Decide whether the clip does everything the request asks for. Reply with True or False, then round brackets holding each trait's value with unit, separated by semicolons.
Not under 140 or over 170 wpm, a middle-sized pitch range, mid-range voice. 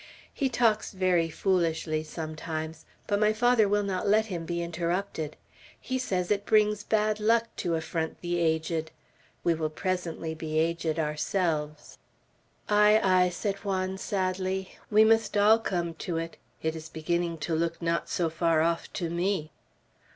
True (155 wpm; 3.9 semitones; 175 Hz)